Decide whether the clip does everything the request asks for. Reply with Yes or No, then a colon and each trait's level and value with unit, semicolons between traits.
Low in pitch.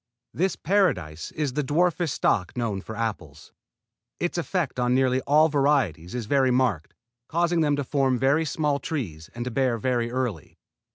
Yes: low, 130 Hz